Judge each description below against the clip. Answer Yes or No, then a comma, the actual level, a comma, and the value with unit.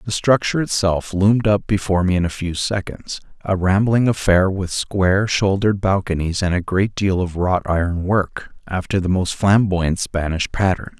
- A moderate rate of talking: Yes, average, 175 wpm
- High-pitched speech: No, very low, 95 Hz